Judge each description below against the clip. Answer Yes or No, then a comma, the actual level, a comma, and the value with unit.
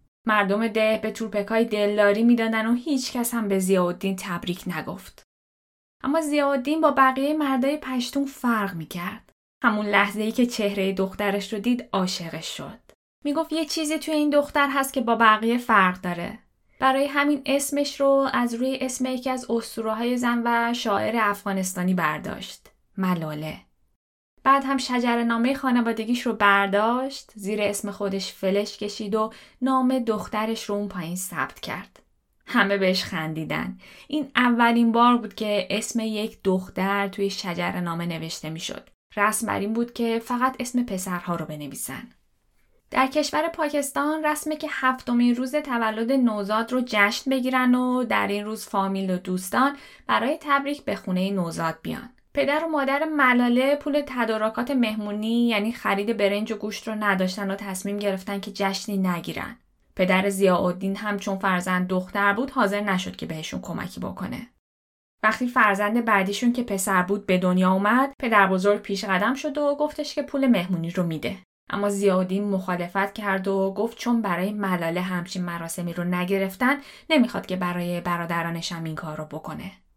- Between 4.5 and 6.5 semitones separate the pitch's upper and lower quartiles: Yes, average, 4.8 semitones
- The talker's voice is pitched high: Yes, high, 215 Hz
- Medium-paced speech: No, fast, 160 wpm